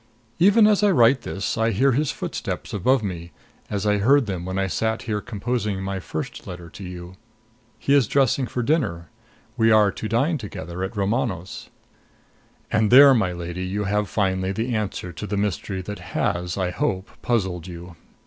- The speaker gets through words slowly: No, average, 180 wpm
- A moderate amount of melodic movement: Yes, average, 4.4 semitones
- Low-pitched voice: Yes, low, 105 Hz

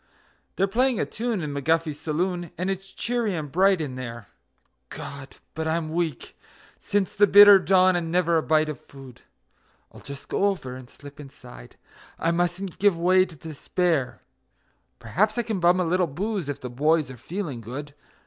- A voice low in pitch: No, medium, 165 Hz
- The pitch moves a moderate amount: Yes, average, 4.8 semitones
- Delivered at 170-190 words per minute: Yes, average, 175 wpm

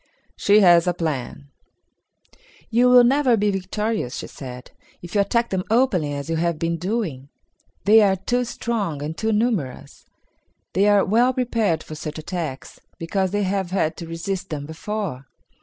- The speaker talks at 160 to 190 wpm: Yes, average, 165 wpm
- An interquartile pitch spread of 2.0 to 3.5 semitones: No, wide, 5.4 semitones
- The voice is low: No, high, 190 Hz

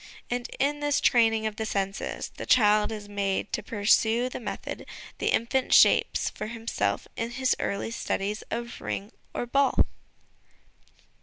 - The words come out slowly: No, average, 150 wpm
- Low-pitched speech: No, high, 225 Hz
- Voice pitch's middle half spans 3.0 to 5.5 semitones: No, narrow, 2.6 semitones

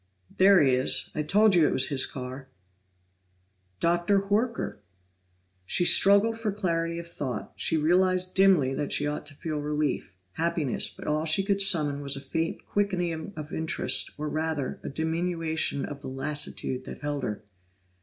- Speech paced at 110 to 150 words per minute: No, average, 165 wpm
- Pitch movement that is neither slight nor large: Yes, average, 4.2 semitones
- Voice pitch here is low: No, medium, 160 Hz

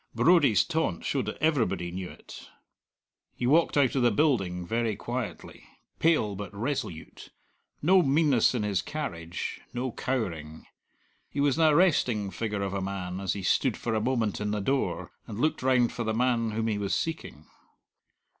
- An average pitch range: No, wide, 5.9 semitones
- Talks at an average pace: Yes, average, 170 wpm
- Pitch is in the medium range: No, low, 115 Hz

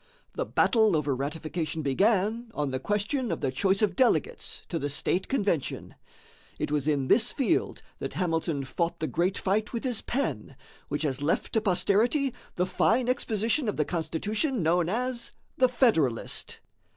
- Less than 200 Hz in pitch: Yes, high, 190 Hz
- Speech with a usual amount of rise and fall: No, wide, 6.9 semitones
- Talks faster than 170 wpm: No, average, 165 wpm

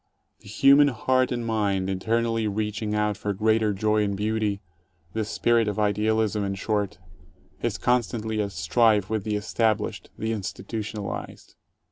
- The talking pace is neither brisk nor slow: Yes, average, 155 wpm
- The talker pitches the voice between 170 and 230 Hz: No, low, 105 Hz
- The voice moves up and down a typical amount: No, narrow, 1.6 semitones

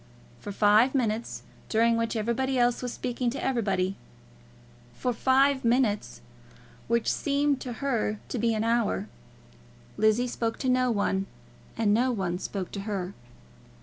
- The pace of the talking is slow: No, average, 145 wpm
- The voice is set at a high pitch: Yes, high, 230 Hz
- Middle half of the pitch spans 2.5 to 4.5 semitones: Yes, average, 3.3 semitones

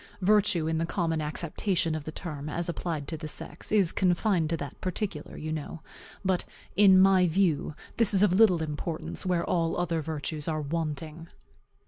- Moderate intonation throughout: Yes, average, 3.0 semitones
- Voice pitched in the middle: Yes, medium, 165 Hz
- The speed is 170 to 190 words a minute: Yes, average, 175 wpm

